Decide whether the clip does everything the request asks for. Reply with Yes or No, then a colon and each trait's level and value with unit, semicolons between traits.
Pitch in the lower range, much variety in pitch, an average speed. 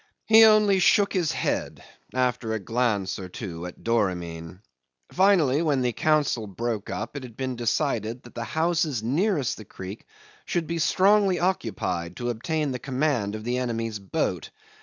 Yes: low, 125 Hz; wide, 6.6 semitones; average, 160 wpm